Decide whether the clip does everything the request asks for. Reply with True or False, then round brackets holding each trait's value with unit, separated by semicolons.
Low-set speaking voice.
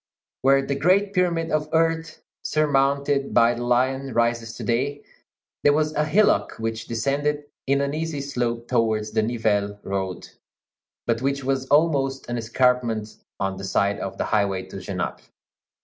True (130 Hz)